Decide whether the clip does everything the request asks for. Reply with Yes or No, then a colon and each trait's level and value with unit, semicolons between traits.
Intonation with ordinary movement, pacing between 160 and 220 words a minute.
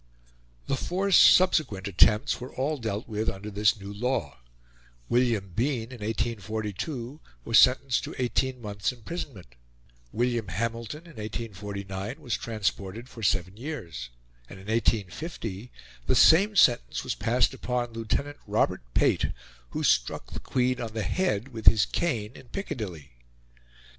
No: average, 4.0 semitones; average, 140 wpm